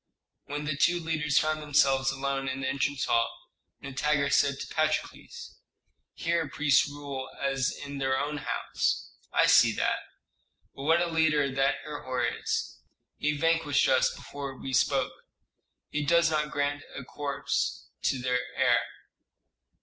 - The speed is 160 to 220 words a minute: No, average, 145 wpm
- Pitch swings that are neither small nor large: No, narrow, 2.0 semitones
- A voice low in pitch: No, medium, 145 Hz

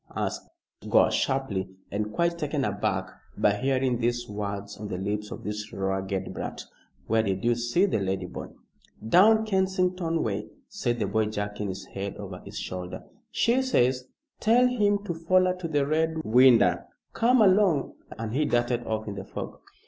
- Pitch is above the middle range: No, low, 120 Hz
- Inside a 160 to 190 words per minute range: Yes, average, 170 wpm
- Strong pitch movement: Yes, wide, 8.8 semitones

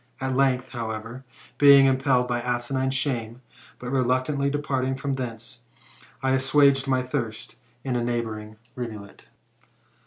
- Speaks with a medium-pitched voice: No, low, 130 Hz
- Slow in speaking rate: Yes, slow, 130 wpm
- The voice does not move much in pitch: Yes, narrow, 2.2 semitones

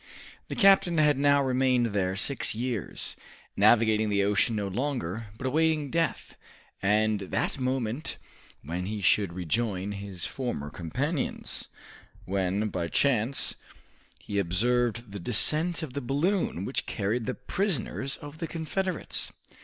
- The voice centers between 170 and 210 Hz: No, low, 120 Hz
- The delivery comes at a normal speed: No, slow, 130 wpm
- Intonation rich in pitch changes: Yes, wide, 6.0 semitones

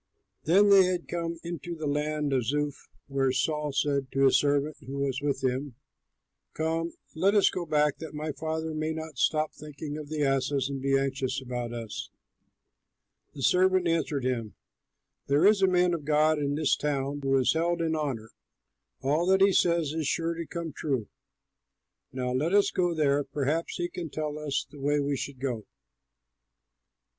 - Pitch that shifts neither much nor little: Yes, average, 3.1 semitones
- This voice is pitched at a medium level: Yes, medium, 150 Hz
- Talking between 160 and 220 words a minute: Yes, average, 175 wpm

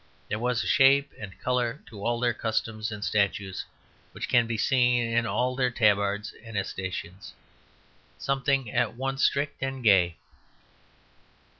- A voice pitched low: Yes, low, 115 Hz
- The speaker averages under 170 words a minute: Yes, average, 145 wpm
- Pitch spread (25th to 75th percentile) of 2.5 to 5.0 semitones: Yes, average, 3.5 semitones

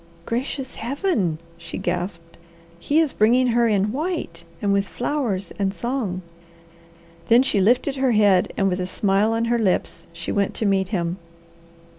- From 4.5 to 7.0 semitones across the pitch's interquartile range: Yes, average, 4.8 semitones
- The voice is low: No, high, 210 Hz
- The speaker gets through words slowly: No, average, 160 wpm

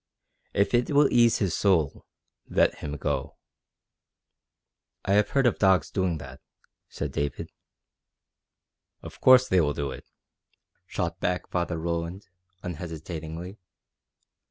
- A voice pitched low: Yes, very low, 90 Hz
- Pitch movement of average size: Yes, average, 4.1 semitones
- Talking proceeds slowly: Yes, slow, 120 wpm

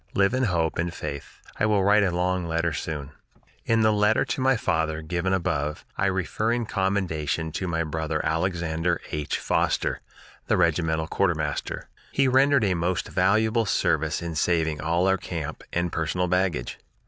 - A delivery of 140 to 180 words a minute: Yes, average, 165 wpm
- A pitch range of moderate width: Yes, average, 3.5 semitones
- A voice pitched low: Yes, very low, 85 Hz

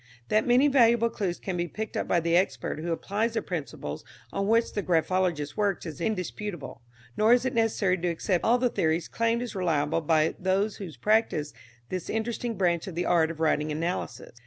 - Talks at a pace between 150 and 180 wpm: No, average, 195 wpm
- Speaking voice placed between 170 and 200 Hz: Yes, medium, 185 Hz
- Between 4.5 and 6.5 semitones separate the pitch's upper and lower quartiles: Yes, average, 5.0 semitones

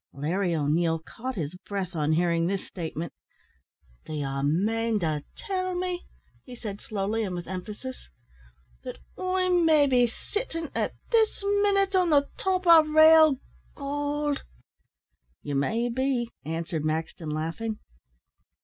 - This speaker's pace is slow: Yes, slow, 125 wpm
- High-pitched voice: Yes, high, 225 Hz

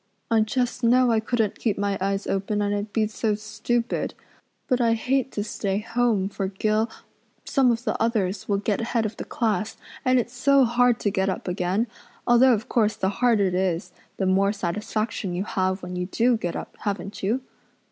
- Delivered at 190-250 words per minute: Yes, average, 200 wpm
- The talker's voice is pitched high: Yes, high, 215 Hz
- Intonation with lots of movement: No, average, 3.2 semitones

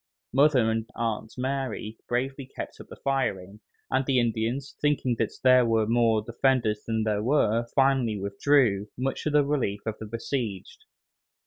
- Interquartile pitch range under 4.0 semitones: Yes, average, 3.5 semitones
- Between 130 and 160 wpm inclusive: Yes, average, 155 wpm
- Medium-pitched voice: No, low, 120 Hz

